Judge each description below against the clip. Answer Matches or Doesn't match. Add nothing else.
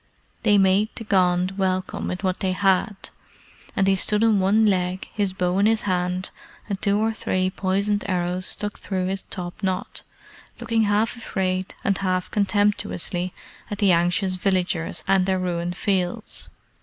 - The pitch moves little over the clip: Matches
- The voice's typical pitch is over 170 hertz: Matches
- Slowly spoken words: Doesn't match